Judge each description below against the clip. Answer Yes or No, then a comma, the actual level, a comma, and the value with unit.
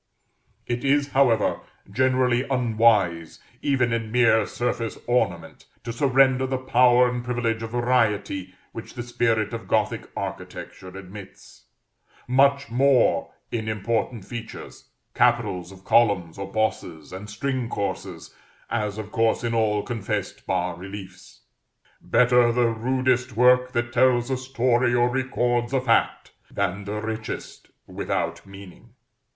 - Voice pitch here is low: Yes, low, 115 Hz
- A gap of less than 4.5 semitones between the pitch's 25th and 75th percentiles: Yes, average, 3.1 semitones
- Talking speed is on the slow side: Yes, slow, 130 wpm